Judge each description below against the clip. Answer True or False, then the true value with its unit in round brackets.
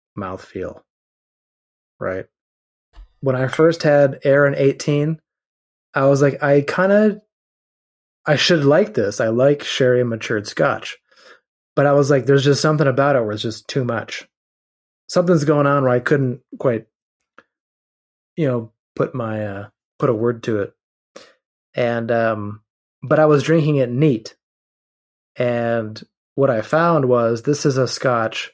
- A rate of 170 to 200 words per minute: False (150 wpm)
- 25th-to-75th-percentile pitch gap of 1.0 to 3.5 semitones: False (4.1 semitones)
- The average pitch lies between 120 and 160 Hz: True (135 Hz)